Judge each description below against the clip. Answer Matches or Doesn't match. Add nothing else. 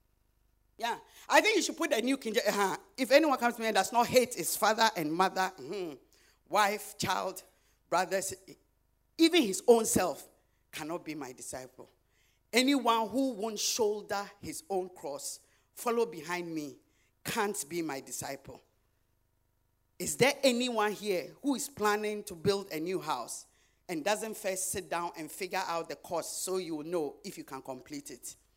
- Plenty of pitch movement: Matches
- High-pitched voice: Matches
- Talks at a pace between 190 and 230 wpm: Doesn't match